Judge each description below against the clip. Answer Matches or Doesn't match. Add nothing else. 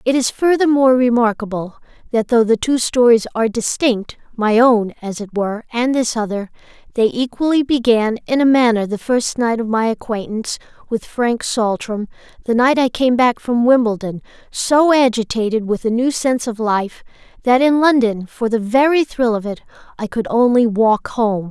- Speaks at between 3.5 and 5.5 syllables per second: Matches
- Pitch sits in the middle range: Doesn't match